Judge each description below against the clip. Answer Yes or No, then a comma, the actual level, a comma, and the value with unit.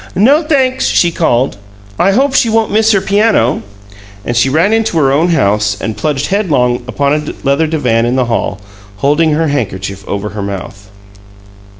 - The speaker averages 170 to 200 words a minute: Yes, average, 175 wpm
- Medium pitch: Yes, medium, 145 Hz